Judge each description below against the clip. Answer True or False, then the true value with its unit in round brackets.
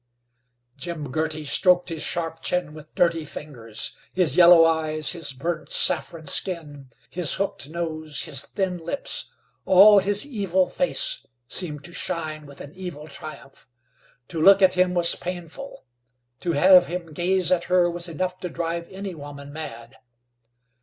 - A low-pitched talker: False (170 Hz)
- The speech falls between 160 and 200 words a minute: False (150 wpm)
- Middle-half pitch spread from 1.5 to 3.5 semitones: True (2.9 semitones)